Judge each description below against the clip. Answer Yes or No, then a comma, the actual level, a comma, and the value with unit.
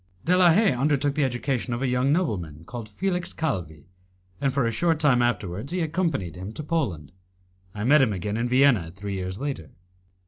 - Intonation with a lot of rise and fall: Yes, wide, 7.1 semitones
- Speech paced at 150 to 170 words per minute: No, average, 185 wpm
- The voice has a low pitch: Yes, low, 125 Hz